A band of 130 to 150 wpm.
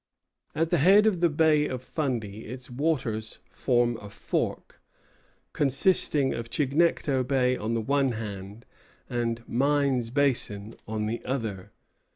Yes: slow, 135 wpm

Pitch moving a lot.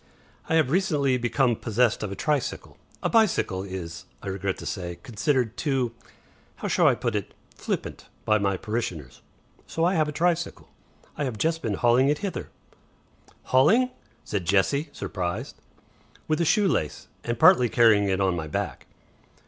Yes: wide, 7.3 semitones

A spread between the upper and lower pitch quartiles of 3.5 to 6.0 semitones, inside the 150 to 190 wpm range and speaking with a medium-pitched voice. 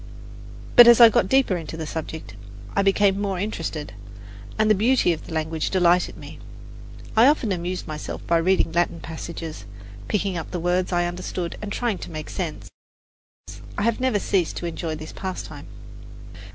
Yes: average, 3.8 semitones; average, 165 wpm; medium, 180 Hz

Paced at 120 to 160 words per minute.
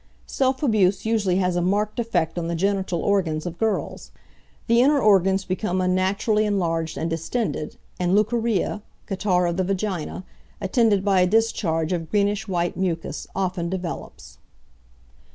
Yes: average, 145 wpm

